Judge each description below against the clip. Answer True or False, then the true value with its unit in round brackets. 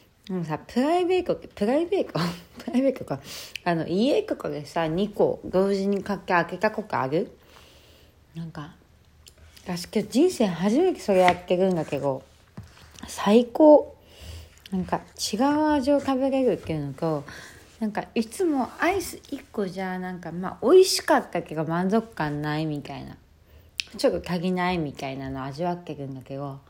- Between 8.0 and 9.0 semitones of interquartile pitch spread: True (8.3 semitones)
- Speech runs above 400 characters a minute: False (310 characters per minute)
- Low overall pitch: False (180 Hz)